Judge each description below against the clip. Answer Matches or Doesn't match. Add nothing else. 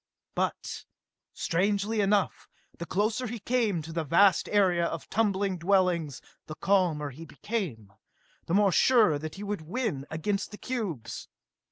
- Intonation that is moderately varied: Matches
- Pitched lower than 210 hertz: Matches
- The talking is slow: Doesn't match